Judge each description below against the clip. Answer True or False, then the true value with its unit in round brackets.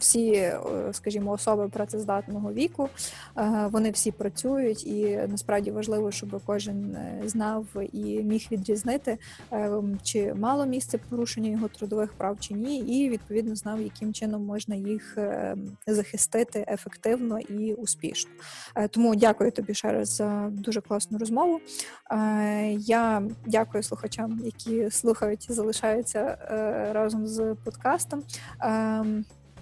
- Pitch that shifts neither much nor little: False (1.4 semitones)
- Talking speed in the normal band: True (115 wpm)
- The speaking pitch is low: False (215 Hz)